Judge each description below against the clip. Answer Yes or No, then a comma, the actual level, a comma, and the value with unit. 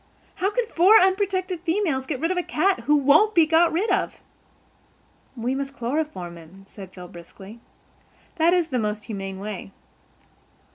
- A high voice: Yes, very high, 300 Hz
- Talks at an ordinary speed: Yes, average, 160 wpm